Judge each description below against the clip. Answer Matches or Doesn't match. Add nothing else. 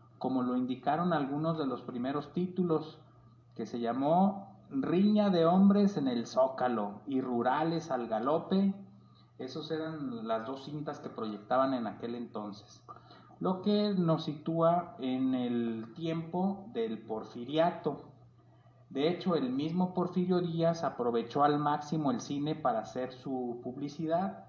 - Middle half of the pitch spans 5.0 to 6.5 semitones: Matches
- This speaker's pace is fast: Doesn't match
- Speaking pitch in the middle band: Matches